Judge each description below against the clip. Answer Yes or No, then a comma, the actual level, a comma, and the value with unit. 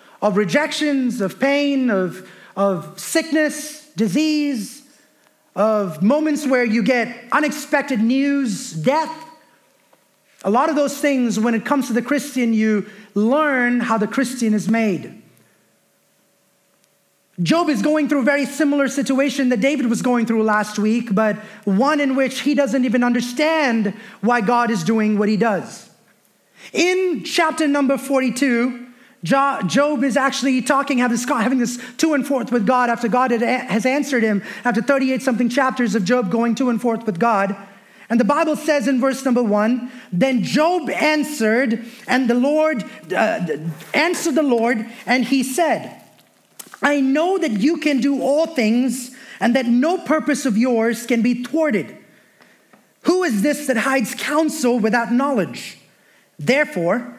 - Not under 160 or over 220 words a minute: No, average, 150 wpm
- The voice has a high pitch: Yes, very high, 255 Hz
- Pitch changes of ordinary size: Yes, average, 3.8 semitones